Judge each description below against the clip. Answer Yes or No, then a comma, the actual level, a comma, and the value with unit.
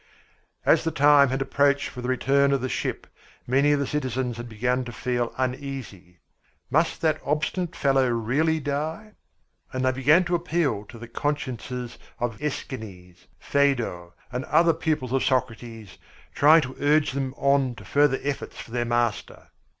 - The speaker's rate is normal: Yes, average, 160 wpm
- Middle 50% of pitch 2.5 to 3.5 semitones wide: Yes, average, 3.2 semitones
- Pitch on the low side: Yes, low, 130 Hz